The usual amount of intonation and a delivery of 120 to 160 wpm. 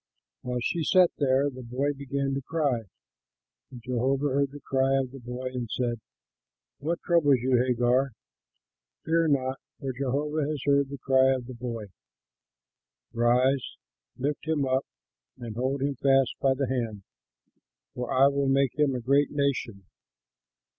No: narrow, 2.0 semitones; average, 155 wpm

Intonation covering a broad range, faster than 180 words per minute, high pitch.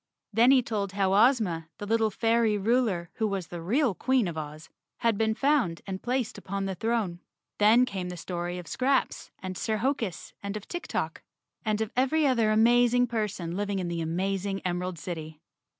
No: average, 4.6 semitones; average, 190 wpm; high, 205 Hz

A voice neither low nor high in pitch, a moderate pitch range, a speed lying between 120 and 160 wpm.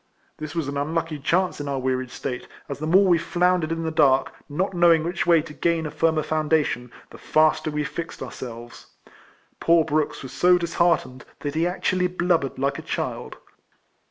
No: medium, 155 Hz; average, 3.1 semitones; average, 190 wpm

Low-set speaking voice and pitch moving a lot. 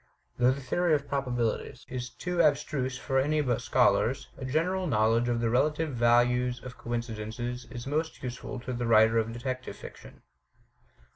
No: low, 125 Hz; average, 2.9 semitones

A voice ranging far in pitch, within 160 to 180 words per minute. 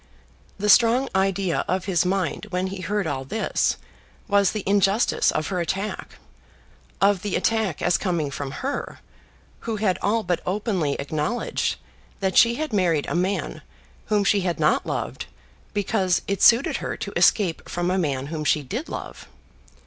No: average, 3.2 semitones; average, 165 wpm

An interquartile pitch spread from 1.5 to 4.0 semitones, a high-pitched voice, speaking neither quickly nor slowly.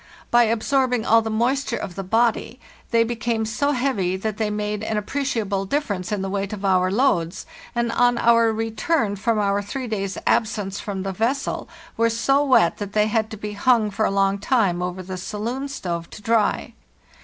Yes: average, 3.1 semitones; high, 215 Hz; average, 195 wpm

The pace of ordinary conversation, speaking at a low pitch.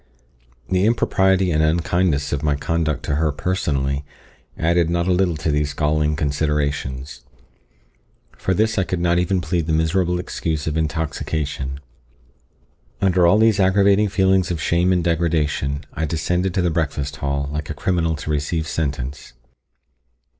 Yes: average, 155 wpm; very low, 80 Hz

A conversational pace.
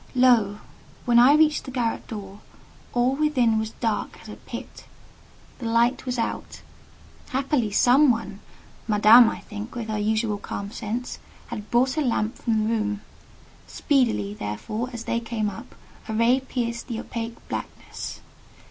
Yes: average, 150 wpm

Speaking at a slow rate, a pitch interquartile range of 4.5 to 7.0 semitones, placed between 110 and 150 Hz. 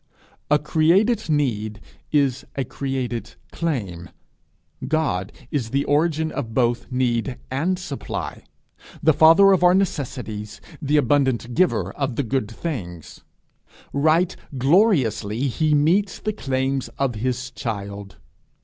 Yes: slow, 120 wpm; average, 5.2 semitones; low, 135 Hz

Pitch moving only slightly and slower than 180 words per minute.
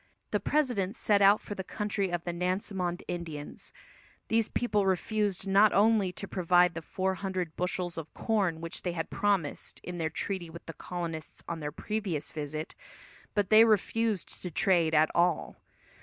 No: average, 3.3 semitones; average, 170 wpm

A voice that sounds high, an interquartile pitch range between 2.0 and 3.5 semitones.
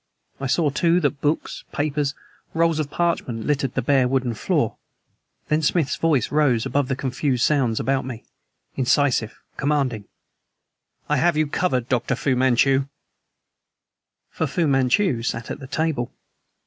No: medium, 140 Hz; average, 3.2 semitones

